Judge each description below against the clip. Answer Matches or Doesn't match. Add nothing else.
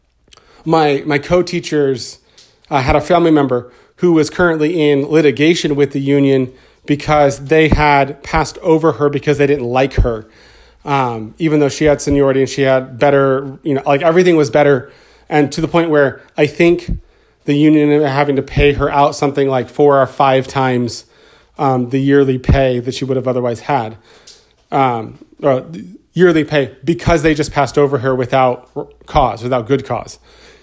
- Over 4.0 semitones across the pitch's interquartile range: Doesn't match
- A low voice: Doesn't match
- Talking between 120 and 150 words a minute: Doesn't match